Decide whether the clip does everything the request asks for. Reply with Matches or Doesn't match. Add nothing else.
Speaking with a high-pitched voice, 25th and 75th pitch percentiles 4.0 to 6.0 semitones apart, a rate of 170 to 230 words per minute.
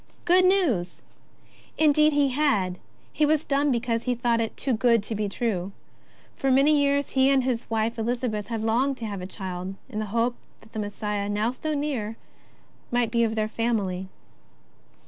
Matches